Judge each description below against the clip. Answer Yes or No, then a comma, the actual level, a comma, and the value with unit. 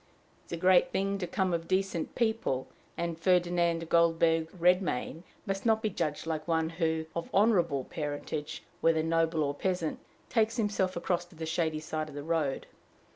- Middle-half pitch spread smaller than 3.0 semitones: Yes, narrow, 2.6 semitones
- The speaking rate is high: No, average, 175 wpm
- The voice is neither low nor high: Yes, medium, 170 Hz